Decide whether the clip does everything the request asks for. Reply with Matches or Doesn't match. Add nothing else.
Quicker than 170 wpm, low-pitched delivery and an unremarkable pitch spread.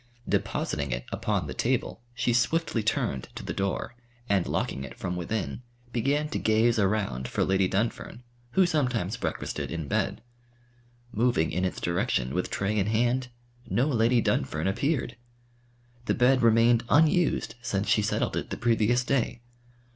Doesn't match